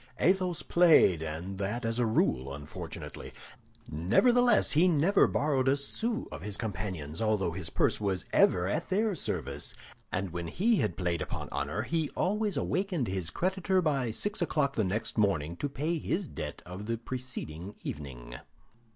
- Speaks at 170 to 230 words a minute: No, average, 160 wpm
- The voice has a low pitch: Yes, low, 115 Hz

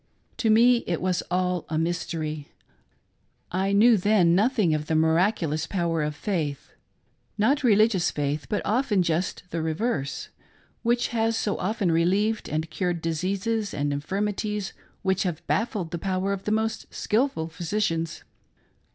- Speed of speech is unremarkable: Yes, average, 145 wpm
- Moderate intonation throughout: Yes, average, 4.7 semitones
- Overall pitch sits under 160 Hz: No, medium, 185 Hz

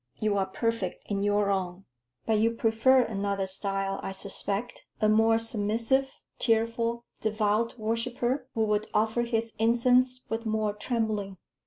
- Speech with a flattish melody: Yes, narrow, 2.2 semitones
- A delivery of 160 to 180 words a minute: No, average, 140 wpm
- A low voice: No, high, 220 Hz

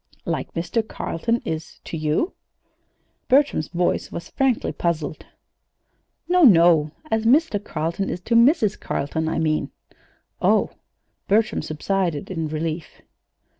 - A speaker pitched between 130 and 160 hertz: No, medium, 175 Hz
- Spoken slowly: Yes, slow, 120 wpm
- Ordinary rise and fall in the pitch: No, wide, 6.1 semitones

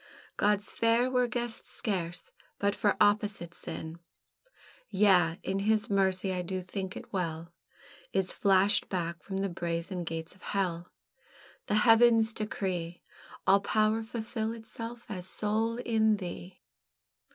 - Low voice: No, high, 200 Hz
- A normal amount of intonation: Yes, average, 3.4 semitones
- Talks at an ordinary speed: No, slow, 130 wpm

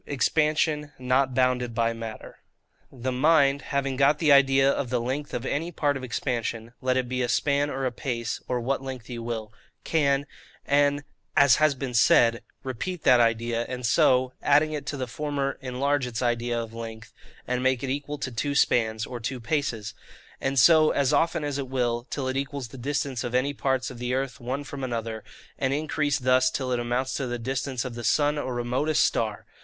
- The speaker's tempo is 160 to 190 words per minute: No, average, 200 wpm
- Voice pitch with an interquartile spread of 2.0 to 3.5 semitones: Yes, average, 2.8 semitones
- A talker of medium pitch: No, low, 130 Hz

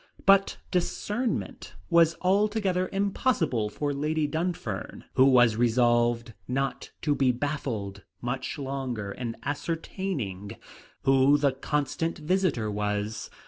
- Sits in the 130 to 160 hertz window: Yes, low, 135 Hz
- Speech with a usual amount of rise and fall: No, wide, 6.1 semitones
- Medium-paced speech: No, slow, 105 wpm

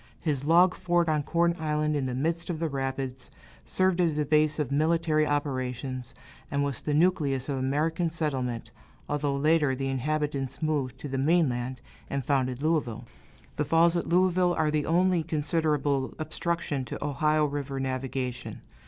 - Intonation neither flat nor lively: Yes, average, 3.3 semitones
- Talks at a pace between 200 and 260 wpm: No, average, 160 wpm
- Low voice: No, medium, 150 Hz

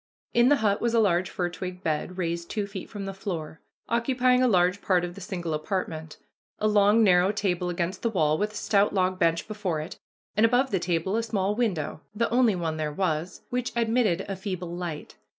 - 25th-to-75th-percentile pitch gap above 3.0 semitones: Yes, average, 3.7 semitones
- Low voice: No, high, 190 Hz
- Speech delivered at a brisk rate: Yes, fast, 210 wpm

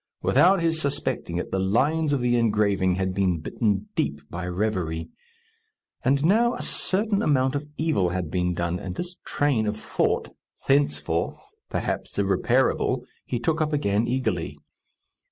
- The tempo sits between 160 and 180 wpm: No, average, 150 wpm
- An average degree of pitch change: No, wide, 7.8 semitones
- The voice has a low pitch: Yes, low, 115 Hz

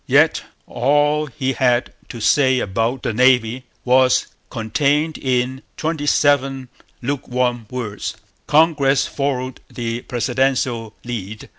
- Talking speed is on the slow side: Yes, slow, 110 wpm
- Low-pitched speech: Yes, low, 130 Hz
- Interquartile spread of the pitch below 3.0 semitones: Yes, narrow, 2.5 semitones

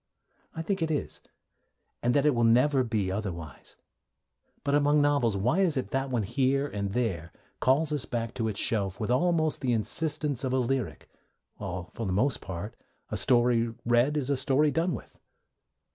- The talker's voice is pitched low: Yes, low, 125 Hz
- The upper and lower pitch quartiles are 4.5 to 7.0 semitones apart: Yes, average, 4.8 semitones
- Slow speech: No, average, 180 wpm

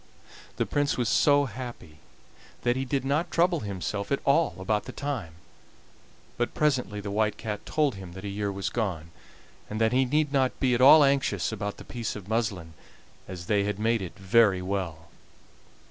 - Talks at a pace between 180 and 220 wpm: Yes, average, 185 wpm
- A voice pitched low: Yes, low, 110 Hz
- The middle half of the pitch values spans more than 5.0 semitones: Yes, wide, 5.4 semitones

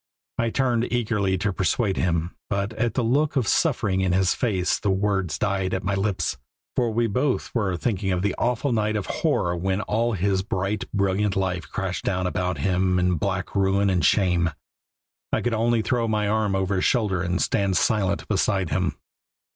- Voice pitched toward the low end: Yes, low, 100 Hz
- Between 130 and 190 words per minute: Yes, average, 185 wpm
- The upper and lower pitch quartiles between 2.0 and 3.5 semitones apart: Yes, average, 2.9 semitones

